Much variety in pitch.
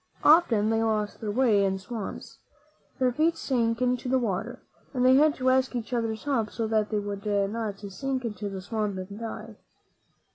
No: average, 3.6 semitones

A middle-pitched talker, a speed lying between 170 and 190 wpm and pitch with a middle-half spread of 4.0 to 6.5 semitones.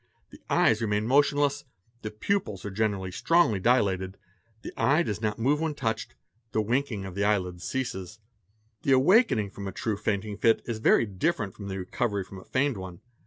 No: low, 110 Hz; average, 180 wpm; average, 5.0 semitones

